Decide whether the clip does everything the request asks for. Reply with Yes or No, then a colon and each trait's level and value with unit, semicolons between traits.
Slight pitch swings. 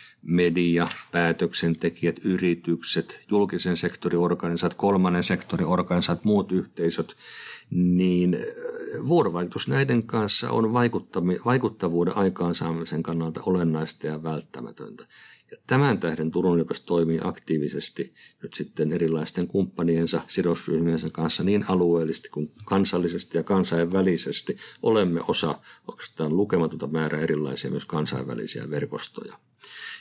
Yes: narrow, 2.2 semitones